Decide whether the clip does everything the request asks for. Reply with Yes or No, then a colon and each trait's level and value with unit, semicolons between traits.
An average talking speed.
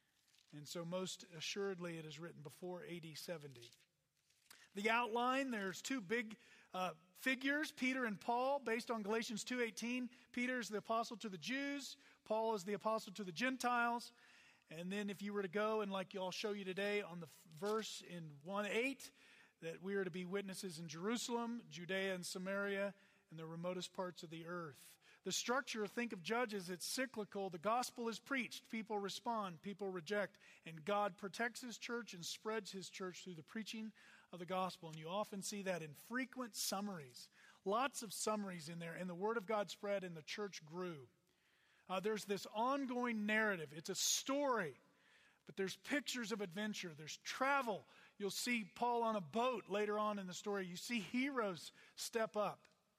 Yes: average, 180 wpm